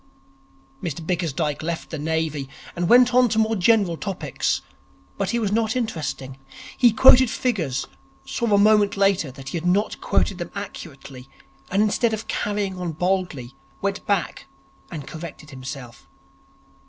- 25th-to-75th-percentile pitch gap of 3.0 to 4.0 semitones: No, wide, 5.5 semitones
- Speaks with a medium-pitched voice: Yes, medium, 180 Hz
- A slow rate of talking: No, average, 150 wpm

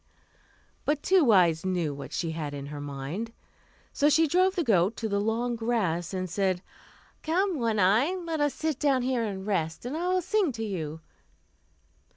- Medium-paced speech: Yes, average, 185 wpm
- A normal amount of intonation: No, wide, 9.0 semitones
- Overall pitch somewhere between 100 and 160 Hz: No, high, 225 Hz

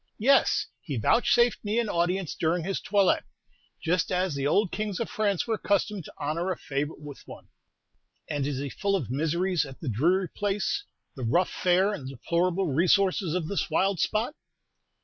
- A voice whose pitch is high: No, medium, 180 Hz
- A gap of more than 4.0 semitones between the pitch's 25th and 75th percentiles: Yes, average, 4.9 semitones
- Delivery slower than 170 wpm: No, average, 175 wpm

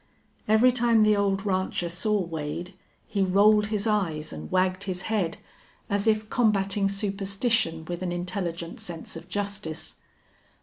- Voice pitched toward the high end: Yes, high, 195 Hz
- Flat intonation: No, average, 3.2 semitones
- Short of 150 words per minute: Yes, average, 140 wpm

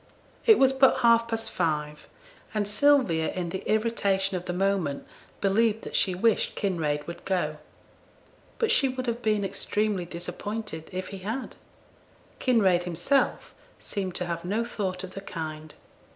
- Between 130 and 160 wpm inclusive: Yes, average, 150 wpm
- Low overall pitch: No, high, 195 Hz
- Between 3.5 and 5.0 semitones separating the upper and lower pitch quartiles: Yes, average, 4.4 semitones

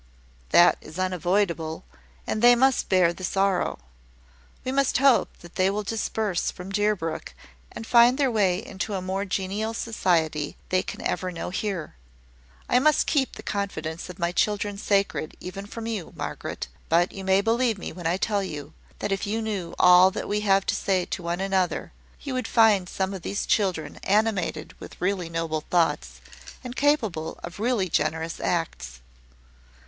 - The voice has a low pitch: No, high, 195 Hz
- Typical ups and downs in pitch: Yes, average, 3.7 semitones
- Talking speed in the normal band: Yes, average, 175 wpm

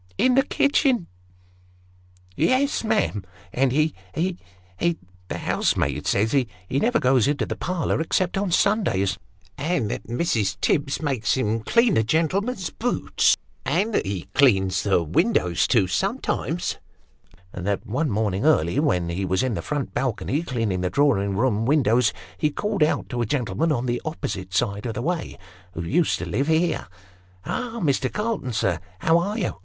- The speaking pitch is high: No, low, 130 Hz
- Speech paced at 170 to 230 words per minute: Yes, average, 175 wpm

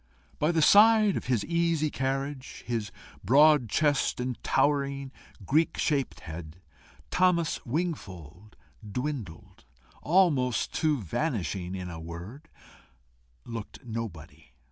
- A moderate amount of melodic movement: No, wide, 7.7 semitones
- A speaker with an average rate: No, slow, 105 wpm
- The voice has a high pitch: No, low, 130 Hz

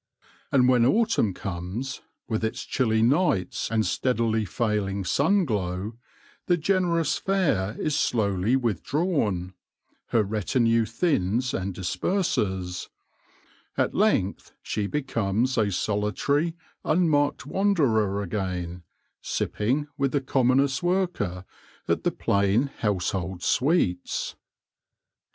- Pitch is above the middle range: No, low, 115 Hz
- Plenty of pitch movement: Yes, wide, 6.8 semitones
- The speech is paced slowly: Yes, slow, 100 wpm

